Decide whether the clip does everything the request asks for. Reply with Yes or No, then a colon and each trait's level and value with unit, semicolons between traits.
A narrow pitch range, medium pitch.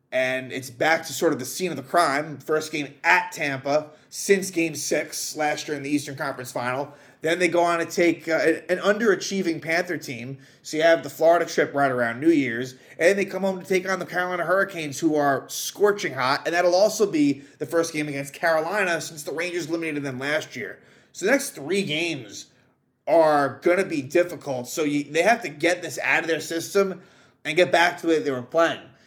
No: average, 3.6 semitones; medium, 160 Hz